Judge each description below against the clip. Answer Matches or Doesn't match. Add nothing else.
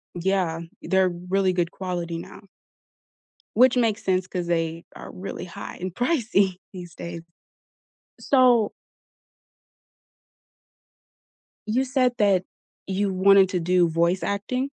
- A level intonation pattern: Doesn't match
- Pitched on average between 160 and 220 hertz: Matches